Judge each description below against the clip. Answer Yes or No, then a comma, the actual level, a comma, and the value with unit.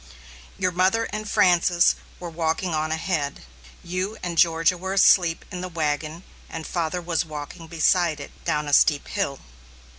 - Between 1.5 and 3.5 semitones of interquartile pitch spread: Yes, narrow, 2.5 semitones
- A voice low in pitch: No, medium, 170 Hz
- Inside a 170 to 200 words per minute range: No, average, 155 wpm